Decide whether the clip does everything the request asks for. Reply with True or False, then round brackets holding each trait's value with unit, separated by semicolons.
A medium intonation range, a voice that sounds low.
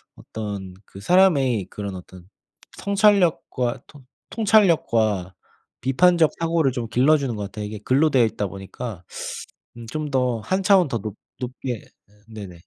False (7.2 semitones; 125 Hz)